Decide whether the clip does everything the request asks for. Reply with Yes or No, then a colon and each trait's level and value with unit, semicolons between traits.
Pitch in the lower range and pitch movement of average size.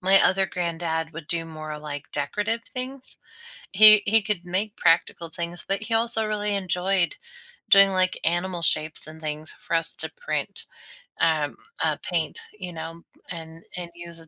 No: medium, 175 Hz; average, 3.4 semitones